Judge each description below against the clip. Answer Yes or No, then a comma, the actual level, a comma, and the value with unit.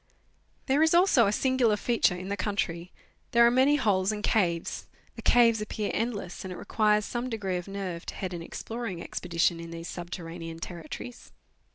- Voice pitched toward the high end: Yes, high, 200 Hz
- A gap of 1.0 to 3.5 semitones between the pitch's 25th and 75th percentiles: No, average, 5.2 semitones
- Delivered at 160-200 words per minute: Yes, average, 180 wpm